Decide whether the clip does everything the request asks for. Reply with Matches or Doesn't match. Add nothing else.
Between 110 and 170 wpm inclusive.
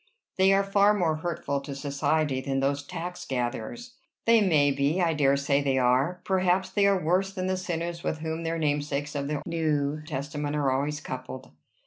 Doesn't match